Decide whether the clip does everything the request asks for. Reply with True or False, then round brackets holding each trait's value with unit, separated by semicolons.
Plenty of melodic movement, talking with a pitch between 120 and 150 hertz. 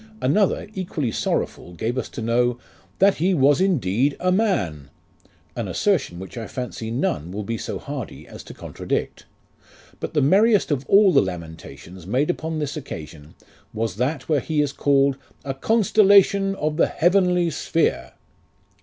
True (8.3 semitones; 140 Hz)